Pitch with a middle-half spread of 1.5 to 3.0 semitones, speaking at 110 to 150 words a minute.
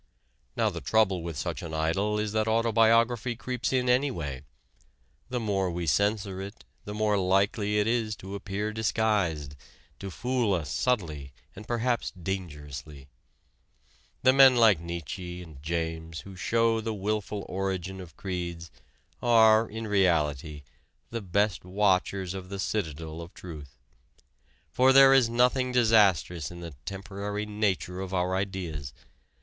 No: average, 4.5 semitones; average, 140 wpm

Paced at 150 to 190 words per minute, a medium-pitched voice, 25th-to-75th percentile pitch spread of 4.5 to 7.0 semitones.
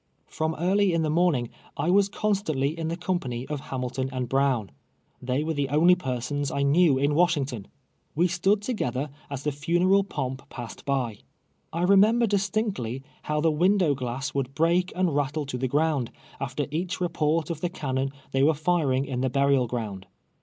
Yes: average, 180 wpm; medium, 150 Hz; average, 4.9 semitones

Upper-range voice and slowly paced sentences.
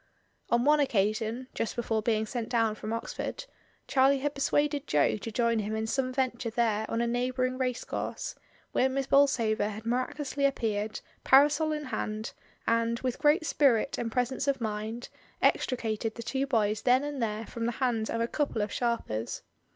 No: high, 235 Hz; average, 175 wpm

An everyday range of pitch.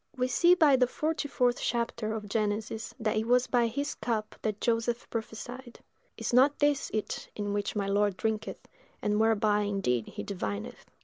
Yes: average, 3.1 semitones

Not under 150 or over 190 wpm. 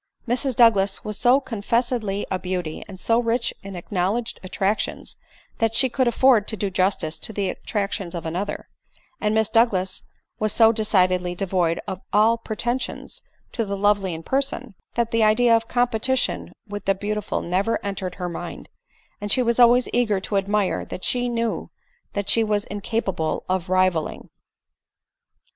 Yes: average, 160 wpm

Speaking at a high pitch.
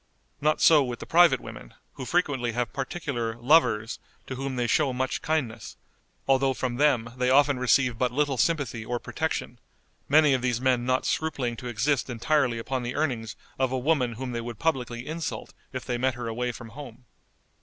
No: low, 130 Hz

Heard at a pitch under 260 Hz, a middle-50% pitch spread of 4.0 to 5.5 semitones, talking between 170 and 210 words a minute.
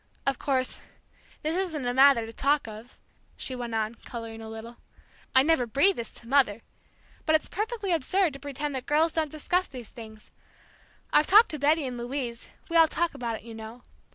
No: very high, 270 Hz; average, 5.1 semitones; average, 195 wpm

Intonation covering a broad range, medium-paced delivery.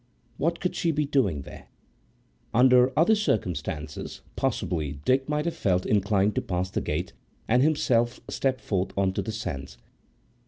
Yes: wide, 7.0 semitones; average, 155 wpm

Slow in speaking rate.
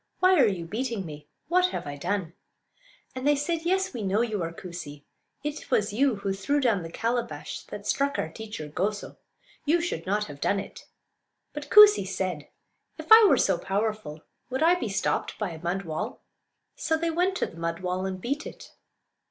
No: average, 195 wpm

